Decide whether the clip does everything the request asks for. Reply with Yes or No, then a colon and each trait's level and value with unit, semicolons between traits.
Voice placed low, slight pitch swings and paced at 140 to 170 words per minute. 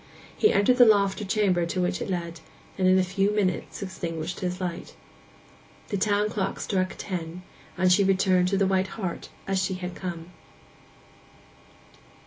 No: medium, 185 Hz; narrow, 1.7 semitones; average, 165 wpm